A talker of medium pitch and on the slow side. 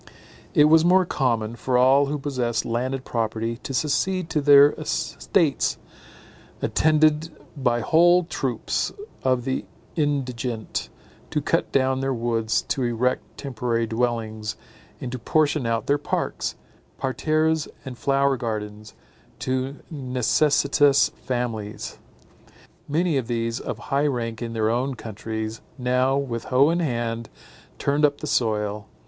No: low, 130 Hz; slow, 130 wpm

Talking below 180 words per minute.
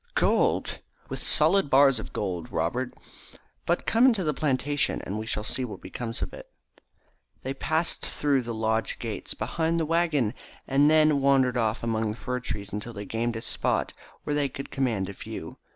No: average, 185 wpm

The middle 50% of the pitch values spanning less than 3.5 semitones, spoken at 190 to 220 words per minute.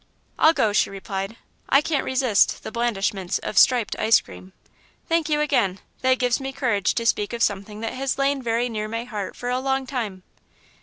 No: average, 4.3 semitones; average, 195 wpm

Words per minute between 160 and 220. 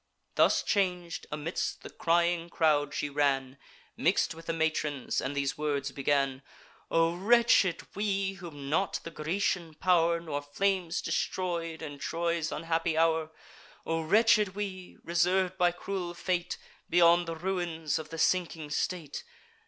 No: slow, 135 wpm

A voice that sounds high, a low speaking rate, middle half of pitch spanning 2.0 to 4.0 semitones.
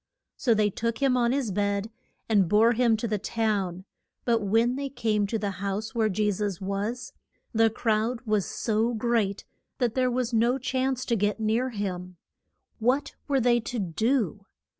No: high, 220 Hz; average, 175 wpm; average, 2.9 semitones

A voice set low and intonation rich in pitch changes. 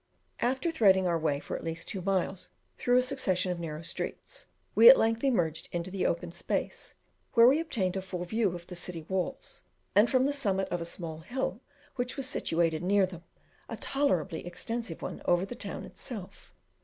No: high, 190 Hz; wide, 5.9 semitones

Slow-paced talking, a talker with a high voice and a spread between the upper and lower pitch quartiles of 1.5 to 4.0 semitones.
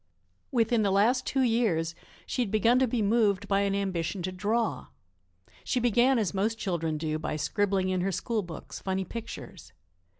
No: average, 175 wpm; high, 200 Hz; average, 3.7 semitones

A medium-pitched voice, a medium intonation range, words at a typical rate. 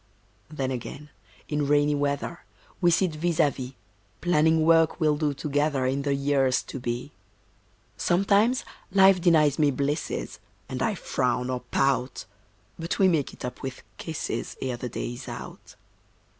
Yes: medium, 145 Hz; average, 3.6 semitones; average, 155 wpm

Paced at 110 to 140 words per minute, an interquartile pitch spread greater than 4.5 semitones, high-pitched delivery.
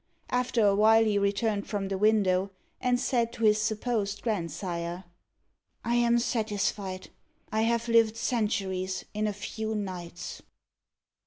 No: slow, 135 wpm; average, 2.7 semitones; high, 210 Hz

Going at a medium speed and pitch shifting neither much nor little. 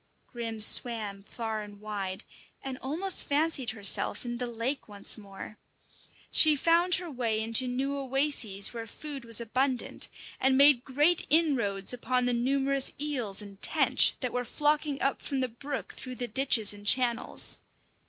Yes: average, 155 wpm; average, 4.0 semitones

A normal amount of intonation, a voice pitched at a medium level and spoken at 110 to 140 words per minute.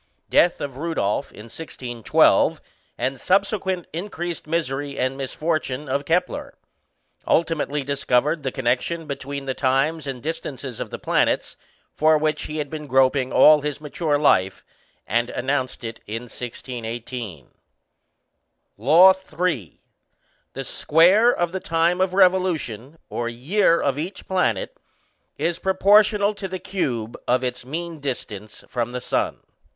Yes: average, 5.0 semitones; medium, 145 Hz; slow, 135 wpm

